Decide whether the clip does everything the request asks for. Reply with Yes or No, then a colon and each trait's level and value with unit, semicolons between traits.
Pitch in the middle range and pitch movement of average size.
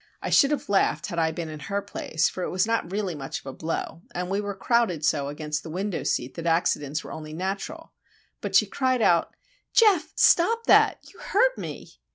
No: medium, 180 Hz; wide, 6.3 semitones